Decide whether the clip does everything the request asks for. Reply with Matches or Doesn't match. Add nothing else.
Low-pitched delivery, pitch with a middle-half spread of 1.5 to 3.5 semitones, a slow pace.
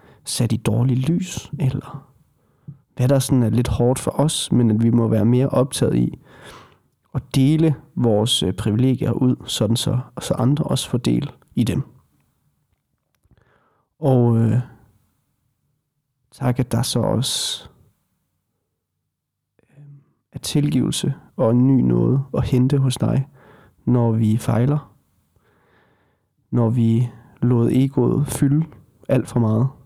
Matches